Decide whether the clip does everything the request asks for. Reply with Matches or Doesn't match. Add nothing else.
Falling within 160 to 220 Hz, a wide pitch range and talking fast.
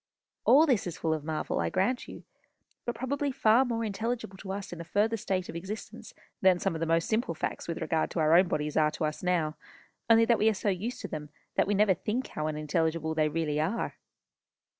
Matches